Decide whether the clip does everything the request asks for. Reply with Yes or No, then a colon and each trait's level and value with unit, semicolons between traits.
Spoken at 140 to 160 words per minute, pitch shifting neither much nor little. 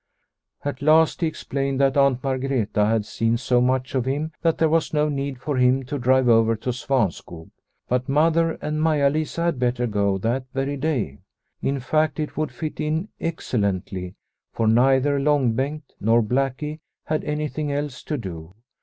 No: average, 175 wpm; average, 3.8 semitones